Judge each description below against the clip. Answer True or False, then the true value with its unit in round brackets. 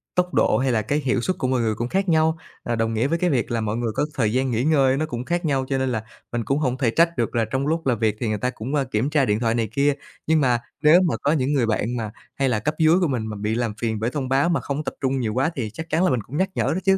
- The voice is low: True (130 Hz)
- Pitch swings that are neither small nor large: True (4.8 semitones)